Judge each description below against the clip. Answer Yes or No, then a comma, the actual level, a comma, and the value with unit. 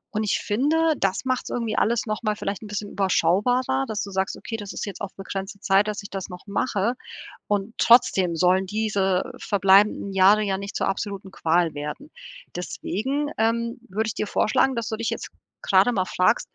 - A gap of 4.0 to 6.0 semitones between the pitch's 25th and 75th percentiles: No, average, 2.9 semitones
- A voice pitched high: Yes, high, 205 Hz